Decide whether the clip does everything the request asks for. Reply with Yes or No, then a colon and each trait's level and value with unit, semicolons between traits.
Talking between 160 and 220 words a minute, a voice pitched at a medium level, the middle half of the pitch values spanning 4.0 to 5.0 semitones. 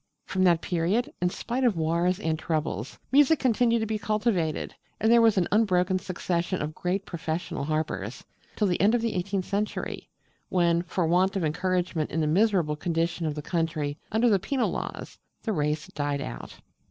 Yes: average, 180 wpm; medium, 180 Hz; average, 4.7 semitones